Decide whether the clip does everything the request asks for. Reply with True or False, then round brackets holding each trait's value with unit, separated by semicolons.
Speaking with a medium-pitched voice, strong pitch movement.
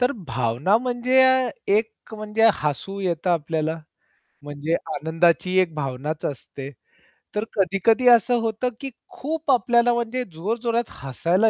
False (205 Hz; 6.9 semitones)